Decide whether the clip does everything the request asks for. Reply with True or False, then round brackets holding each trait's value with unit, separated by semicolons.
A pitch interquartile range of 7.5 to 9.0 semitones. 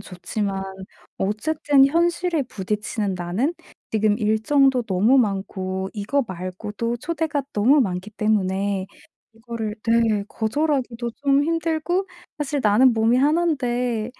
False (5.5 semitones)